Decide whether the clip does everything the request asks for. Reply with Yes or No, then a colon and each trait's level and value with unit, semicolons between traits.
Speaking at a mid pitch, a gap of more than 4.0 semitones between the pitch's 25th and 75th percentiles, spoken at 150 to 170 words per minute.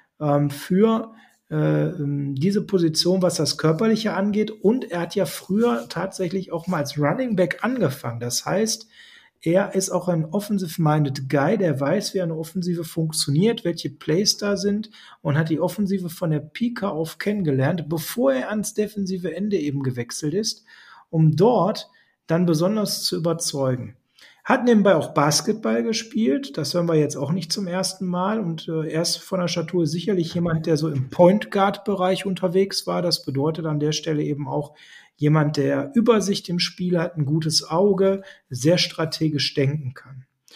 Yes: medium, 175 Hz; average, 4.6 semitones; average, 165 wpm